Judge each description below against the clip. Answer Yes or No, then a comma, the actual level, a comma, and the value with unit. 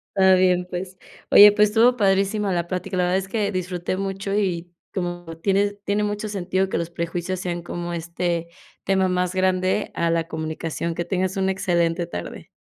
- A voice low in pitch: No, medium, 185 Hz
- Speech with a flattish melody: Yes, narrow, 2.0 semitones